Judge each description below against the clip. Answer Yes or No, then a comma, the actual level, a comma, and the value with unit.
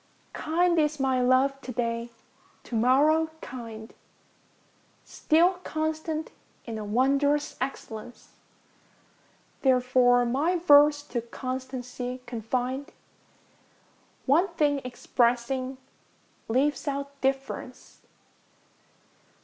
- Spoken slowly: Yes, slow, 85 wpm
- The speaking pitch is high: Yes, very high, 265 Hz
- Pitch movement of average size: Yes, average, 3.0 semitones